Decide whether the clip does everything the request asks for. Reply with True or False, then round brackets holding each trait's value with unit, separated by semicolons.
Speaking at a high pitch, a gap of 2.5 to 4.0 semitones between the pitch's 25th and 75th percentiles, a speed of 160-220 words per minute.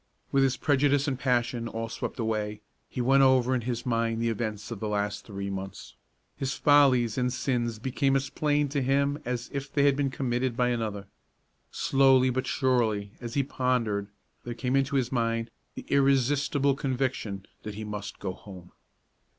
False (125 Hz; 3.3 semitones; 175 wpm)